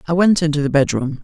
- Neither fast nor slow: No, fast, 245 wpm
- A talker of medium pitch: Yes, medium, 155 Hz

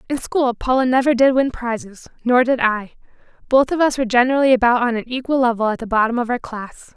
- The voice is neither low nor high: No, high, 245 Hz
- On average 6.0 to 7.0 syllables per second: Yes, 6.1 syllables/s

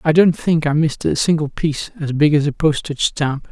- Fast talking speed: Yes, fast, 240 wpm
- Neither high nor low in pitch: Yes, medium, 150 Hz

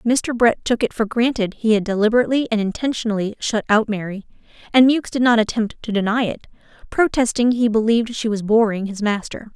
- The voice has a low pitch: No, high, 225 Hz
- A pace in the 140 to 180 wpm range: No, average, 190 wpm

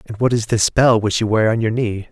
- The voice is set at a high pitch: No, low, 110 Hz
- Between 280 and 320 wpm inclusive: Yes, fast, 310 wpm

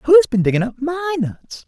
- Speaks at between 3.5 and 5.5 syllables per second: Yes, 5.0 syllables/s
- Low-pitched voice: No, very high, 275 Hz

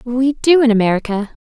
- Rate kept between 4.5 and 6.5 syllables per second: Yes, 5.5 syllables/s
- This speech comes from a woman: Yes, female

